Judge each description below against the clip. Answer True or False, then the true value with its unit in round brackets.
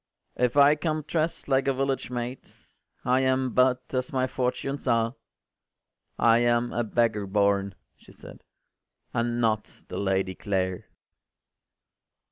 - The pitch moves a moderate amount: True (3.2 semitones)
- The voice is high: False (120 Hz)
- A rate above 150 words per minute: False (135 wpm)